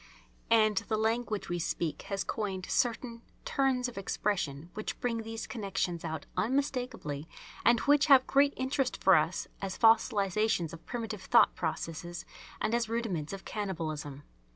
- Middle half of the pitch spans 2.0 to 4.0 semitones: No, average, 5.3 semitones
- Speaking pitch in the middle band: No, high, 215 Hz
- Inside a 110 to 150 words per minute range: Yes, average, 145 wpm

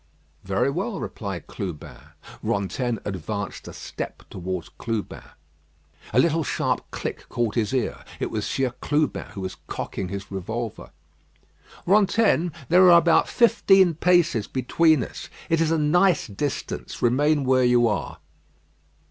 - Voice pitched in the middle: No, low, 130 Hz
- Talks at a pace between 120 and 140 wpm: Yes, slow, 135 wpm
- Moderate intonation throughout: No, wide, 8.2 semitones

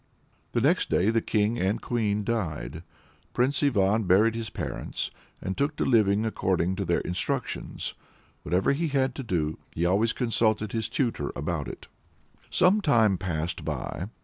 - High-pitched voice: No, low, 110 Hz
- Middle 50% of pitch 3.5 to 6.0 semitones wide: Yes, average, 4.3 semitones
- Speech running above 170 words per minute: No, average, 155 wpm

